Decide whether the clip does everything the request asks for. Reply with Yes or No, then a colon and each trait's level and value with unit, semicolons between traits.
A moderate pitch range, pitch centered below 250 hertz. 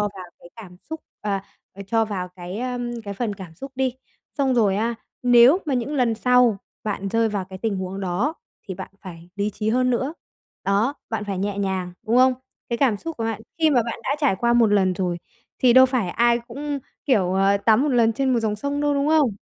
Yes: average, 4.5 semitones; high, 225 Hz